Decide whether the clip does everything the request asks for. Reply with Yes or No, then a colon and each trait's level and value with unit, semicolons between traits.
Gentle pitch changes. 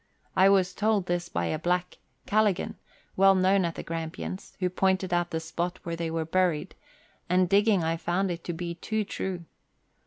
Yes: narrow, 2.3 semitones